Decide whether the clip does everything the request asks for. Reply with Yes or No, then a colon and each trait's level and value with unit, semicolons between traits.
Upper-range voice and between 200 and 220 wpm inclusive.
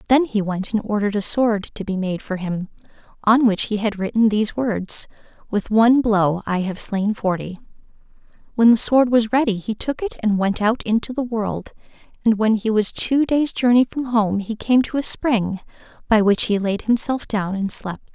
Yes: high, 215 Hz; fast, 205 wpm